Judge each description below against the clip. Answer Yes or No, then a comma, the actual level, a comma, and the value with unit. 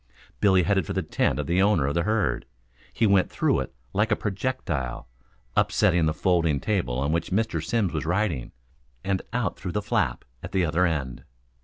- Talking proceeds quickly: No, average, 190 wpm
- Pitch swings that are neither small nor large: Yes, average, 4.9 semitones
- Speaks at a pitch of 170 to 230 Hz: No, very low, 90 Hz